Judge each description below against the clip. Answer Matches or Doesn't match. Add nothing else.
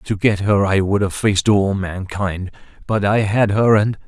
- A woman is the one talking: Doesn't match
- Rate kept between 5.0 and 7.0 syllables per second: Doesn't match